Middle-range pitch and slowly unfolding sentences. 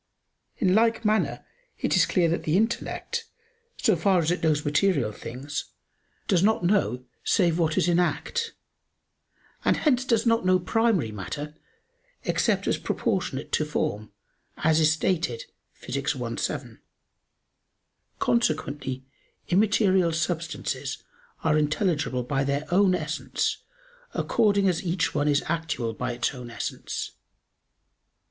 Yes: medium, 170 Hz; slow, 130 wpm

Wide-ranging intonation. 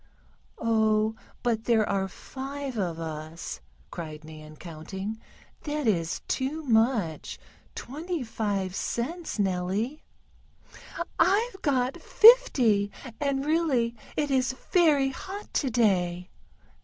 Yes: wide, 7.0 semitones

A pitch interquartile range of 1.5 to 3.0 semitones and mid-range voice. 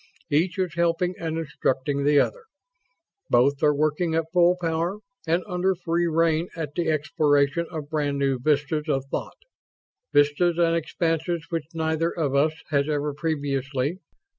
Yes: average, 2.7 semitones; medium, 160 Hz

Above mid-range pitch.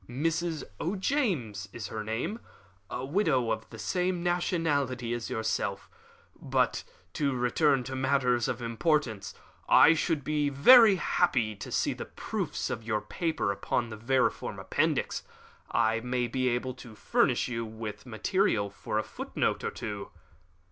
No: low, 125 Hz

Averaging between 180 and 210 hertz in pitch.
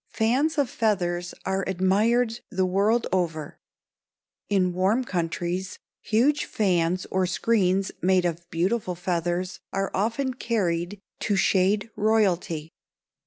Yes: high, 190 Hz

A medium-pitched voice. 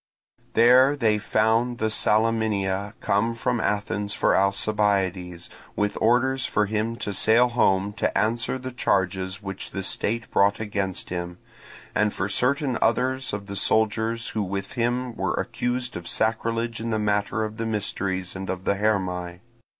No: low, 105 Hz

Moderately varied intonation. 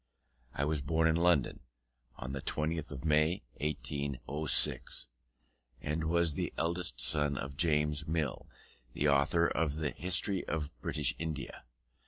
No: narrow, 2.3 semitones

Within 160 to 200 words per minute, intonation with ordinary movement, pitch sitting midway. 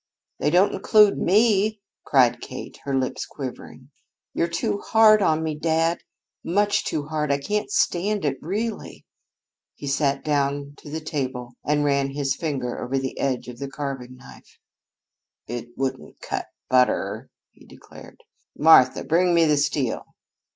No: average, 150 wpm; average, 4.1 semitones; medium, 145 Hz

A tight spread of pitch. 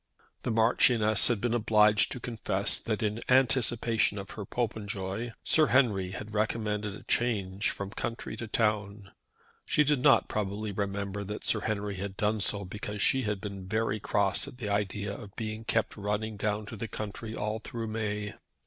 Yes: narrow, 1.8 semitones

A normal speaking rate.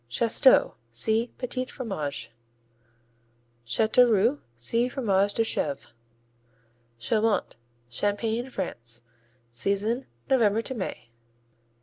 No: slow, 80 wpm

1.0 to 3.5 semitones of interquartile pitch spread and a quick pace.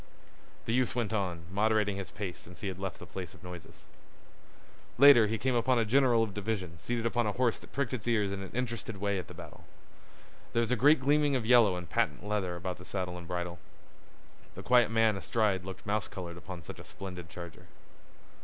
No: average, 4.3 semitones; fast, 210 wpm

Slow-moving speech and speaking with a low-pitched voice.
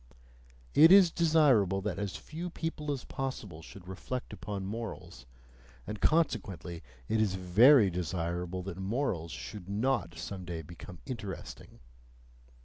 Yes: slow, 130 wpm; low, 100 Hz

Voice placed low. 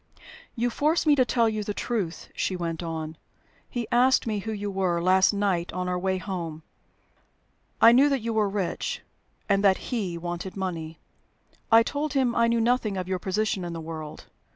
No: high, 200 Hz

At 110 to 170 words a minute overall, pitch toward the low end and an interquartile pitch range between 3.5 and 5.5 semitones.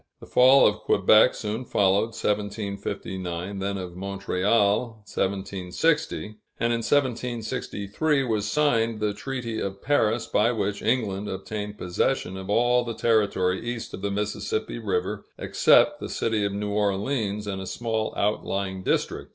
No: average, 140 wpm; low, 105 Hz; average, 2.9 semitones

